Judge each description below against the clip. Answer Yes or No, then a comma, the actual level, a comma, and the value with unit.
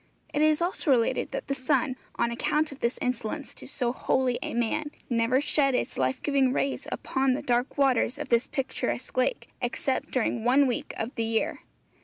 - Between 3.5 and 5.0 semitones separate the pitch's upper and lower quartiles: No, average, 2.9 semitones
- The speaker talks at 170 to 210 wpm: Yes, average, 190 wpm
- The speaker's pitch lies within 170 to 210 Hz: No, very high, 255 Hz